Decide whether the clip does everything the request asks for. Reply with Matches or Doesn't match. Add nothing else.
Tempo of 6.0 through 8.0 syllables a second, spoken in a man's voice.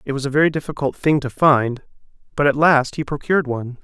Matches